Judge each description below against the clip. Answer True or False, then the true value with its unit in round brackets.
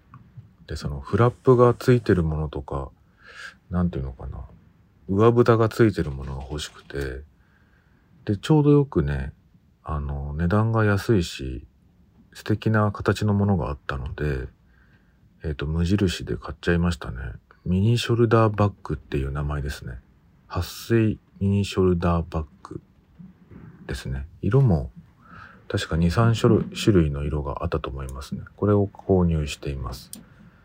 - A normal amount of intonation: False (6.2 semitones)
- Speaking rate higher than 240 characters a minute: True (285 characters per minute)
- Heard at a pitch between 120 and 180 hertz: False (90 Hz)